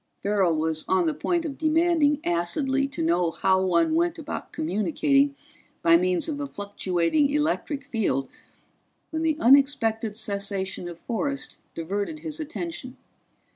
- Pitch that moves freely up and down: Yes, wide, 8.4 semitones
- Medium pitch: No, high, 235 Hz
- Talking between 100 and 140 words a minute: Yes, slow, 135 wpm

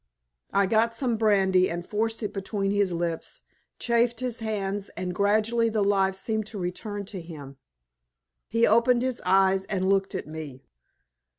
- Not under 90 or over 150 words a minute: No, average, 160 wpm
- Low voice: No, high, 200 Hz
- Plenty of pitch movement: No, average, 3.0 semitones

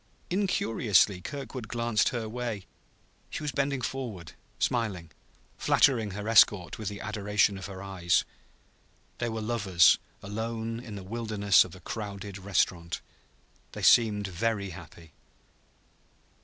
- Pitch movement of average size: Yes, average, 3.2 semitones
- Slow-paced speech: Yes, slow, 125 wpm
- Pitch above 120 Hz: No, low, 105 Hz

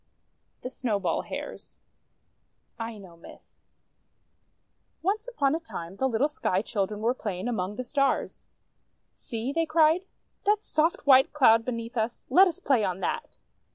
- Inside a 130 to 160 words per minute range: Yes, average, 140 wpm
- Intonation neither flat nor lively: No, wide, 6.2 semitones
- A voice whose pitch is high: Yes, high, 245 Hz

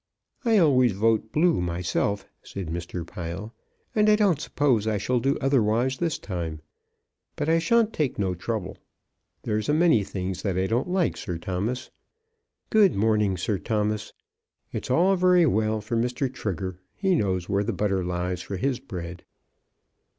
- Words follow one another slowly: No, average, 160 wpm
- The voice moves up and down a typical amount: No, wide, 7.5 semitones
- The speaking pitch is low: Yes, low, 110 Hz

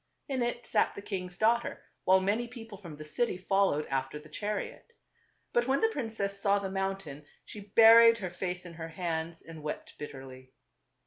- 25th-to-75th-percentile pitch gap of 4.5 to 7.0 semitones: Yes, wide, 5.6 semitones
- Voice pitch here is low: No, high, 195 Hz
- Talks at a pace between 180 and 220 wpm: Yes, average, 185 wpm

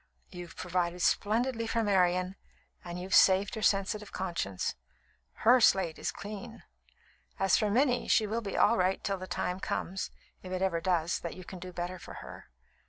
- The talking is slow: No, average, 175 wpm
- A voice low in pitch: No, high, 190 Hz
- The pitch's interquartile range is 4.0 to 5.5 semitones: No, average, 2.9 semitones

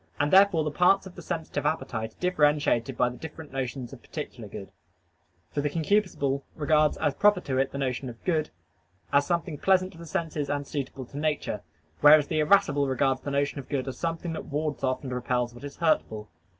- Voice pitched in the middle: Yes, medium, 145 Hz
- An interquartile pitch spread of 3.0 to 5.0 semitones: Yes, average, 3.4 semitones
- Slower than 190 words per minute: No, fast, 205 wpm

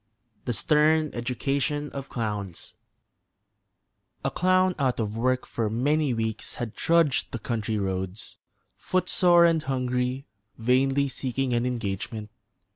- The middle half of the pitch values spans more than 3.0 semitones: Yes, average, 4.6 semitones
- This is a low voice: Yes, low, 125 Hz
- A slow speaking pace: Yes, slow, 120 wpm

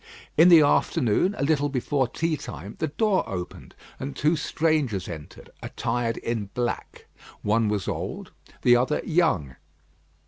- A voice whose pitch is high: No, low, 130 Hz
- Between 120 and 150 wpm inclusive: Yes, average, 140 wpm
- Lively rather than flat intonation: Yes, wide, 6.5 semitones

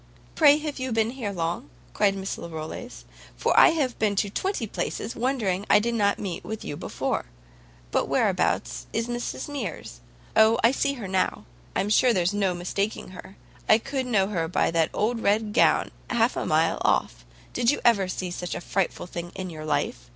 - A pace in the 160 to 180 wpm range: No, average, 190 wpm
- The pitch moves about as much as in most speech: Yes, average, 5.0 semitones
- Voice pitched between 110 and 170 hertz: No, high, 205 Hz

